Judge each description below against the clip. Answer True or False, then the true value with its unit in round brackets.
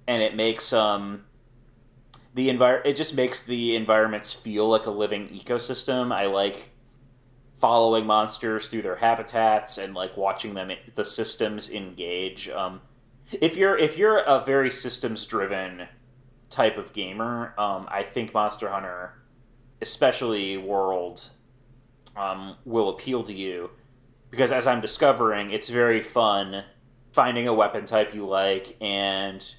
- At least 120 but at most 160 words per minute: True (140 wpm)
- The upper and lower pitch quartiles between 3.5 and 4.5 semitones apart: True (4.1 semitones)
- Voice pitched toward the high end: False (115 Hz)